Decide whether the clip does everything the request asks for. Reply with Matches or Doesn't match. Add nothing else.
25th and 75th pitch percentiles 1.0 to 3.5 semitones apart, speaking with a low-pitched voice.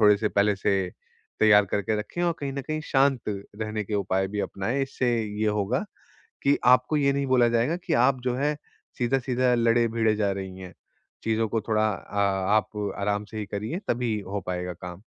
Doesn't match